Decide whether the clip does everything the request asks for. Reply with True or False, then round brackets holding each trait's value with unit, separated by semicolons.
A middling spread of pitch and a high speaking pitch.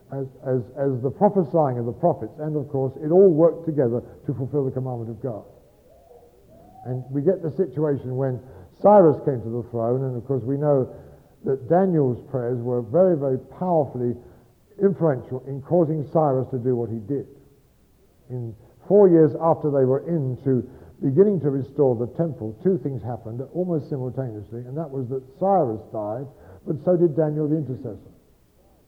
False (4.3 semitones; 135 Hz)